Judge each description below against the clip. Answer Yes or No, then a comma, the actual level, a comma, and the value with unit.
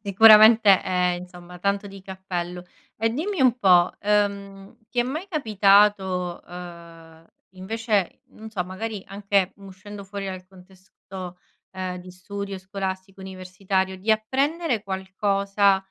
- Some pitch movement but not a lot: No, narrow, 2.0 semitones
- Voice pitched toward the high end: Yes, high, 195 Hz